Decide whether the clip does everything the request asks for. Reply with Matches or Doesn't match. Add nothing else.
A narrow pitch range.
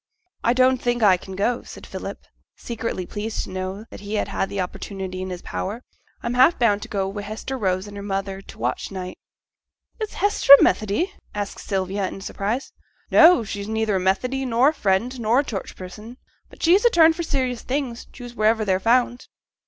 Doesn't match